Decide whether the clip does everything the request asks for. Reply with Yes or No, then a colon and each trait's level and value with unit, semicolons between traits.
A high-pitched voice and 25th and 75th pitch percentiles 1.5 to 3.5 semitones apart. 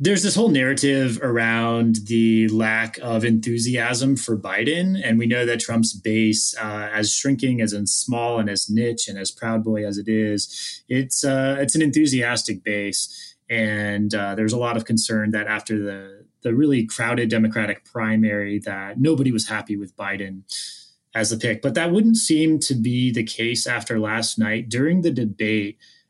No: low, 115 Hz; narrow, 2.6 semitones